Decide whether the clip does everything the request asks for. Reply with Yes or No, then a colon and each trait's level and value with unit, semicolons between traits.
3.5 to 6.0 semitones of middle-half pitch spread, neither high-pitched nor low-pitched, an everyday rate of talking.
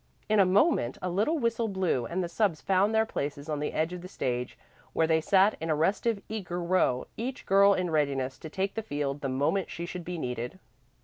No: average, 5.2 semitones; medium, 180 Hz; fast, 225 wpm